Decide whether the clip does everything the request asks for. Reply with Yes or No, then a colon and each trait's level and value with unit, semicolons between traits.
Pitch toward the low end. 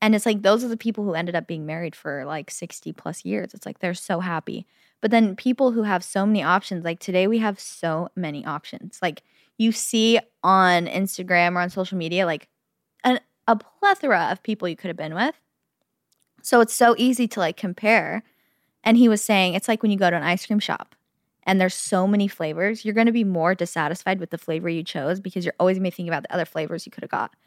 No: high, 190 Hz